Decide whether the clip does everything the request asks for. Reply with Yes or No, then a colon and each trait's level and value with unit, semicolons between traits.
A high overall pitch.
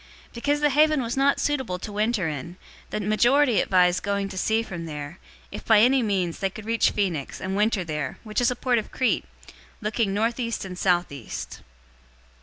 Yes: high, 210 Hz